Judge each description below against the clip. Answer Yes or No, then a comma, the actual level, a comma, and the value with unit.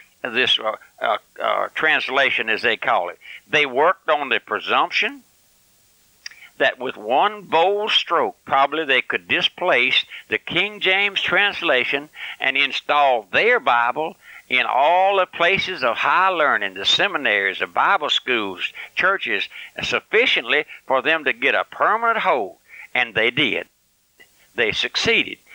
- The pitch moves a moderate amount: Yes, average, 3.6 semitones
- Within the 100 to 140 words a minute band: Yes, slow, 135 wpm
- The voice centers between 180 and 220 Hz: Yes, medium, 185 Hz